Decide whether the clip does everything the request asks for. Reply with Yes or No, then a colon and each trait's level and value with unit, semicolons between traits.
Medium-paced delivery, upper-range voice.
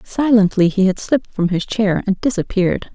Yes: average, 185 wpm; high, 205 Hz